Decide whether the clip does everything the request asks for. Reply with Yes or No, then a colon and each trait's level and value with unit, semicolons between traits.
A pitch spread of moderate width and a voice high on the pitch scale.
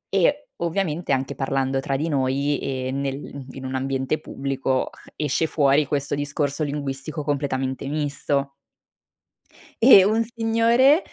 No: average, 3.0 semitones; medium, 140 Hz